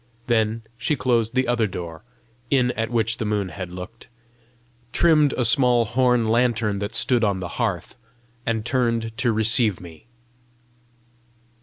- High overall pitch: No, low, 115 Hz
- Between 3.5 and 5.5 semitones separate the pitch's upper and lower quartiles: No, average, 2.8 semitones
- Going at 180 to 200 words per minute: No, average, 145 wpm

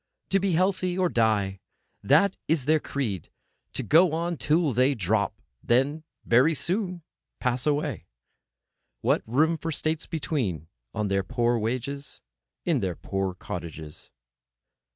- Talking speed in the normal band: No, slow, 125 wpm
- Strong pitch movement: Yes, wide, 7.4 semitones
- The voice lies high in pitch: No, medium, 140 Hz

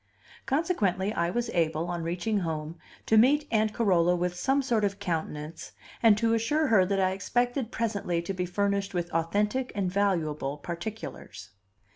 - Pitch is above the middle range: Yes, high, 195 Hz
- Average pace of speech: Yes, average, 160 wpm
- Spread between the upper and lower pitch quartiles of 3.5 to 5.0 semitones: Yes, average, 4.6 semitones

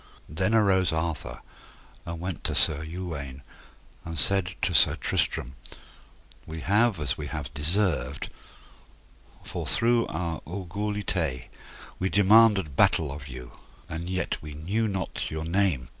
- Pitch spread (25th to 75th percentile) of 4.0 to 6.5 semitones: Yes, average, 4.6 semitones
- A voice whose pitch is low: Yes, very low, 85 Hz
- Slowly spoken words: Yes, slow, 130 wpm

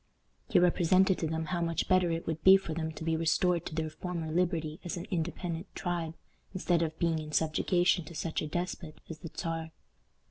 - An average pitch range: No, narrow, 1.8 semitones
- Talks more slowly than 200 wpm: No, fast, 205 wpm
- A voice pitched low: No, medium, 165 Hz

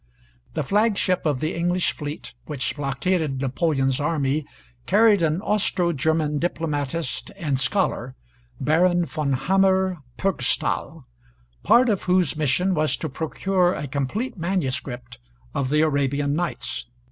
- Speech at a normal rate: No, slow, 125 wpm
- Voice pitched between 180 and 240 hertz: No, medium, 155 Hz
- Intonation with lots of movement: No, average, 4.7 semitones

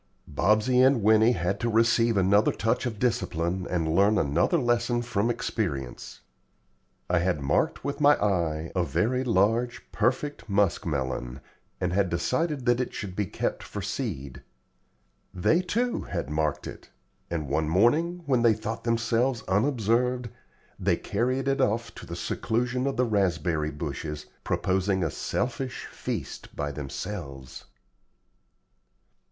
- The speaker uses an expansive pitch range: Yes, wide, 6.3 semitones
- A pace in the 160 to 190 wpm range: No, average, 140 wpm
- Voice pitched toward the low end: Yes, low, 105 Hz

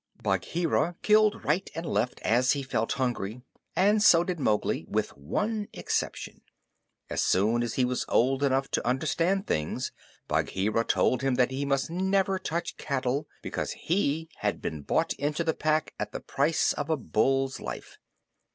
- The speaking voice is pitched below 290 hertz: Yes, medium, 140 Hz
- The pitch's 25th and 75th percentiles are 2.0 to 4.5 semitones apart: No, wide, 5.4 semitones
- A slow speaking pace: No, average, 160 wpm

